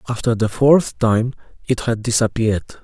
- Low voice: Yes, low, 115 Hz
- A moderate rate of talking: Yes, average, 150 wpm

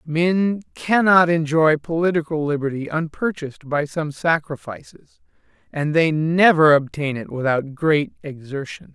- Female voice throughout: No, male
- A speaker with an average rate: No, slow, 115 wpm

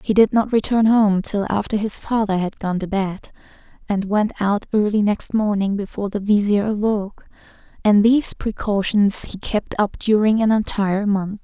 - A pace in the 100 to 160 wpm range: No, average, 175 wpm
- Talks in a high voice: Yes, high, 205 Hz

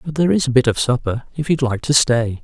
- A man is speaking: Yes, male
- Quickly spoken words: Yes, fast, 295 wpm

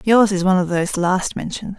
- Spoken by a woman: Yes, female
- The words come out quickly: Yes, fast, 235 wpm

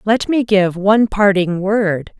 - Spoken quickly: No, average, 165 wpm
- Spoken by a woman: Yes, female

